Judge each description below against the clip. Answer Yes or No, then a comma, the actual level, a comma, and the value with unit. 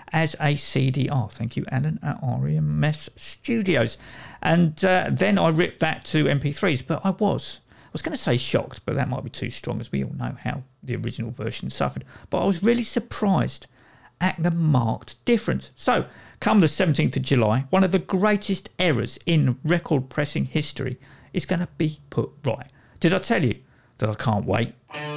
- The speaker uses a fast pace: No, average, 190 wpm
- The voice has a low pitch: No, medium, 150 Hz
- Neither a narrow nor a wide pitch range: No, wide, 5.9 semitones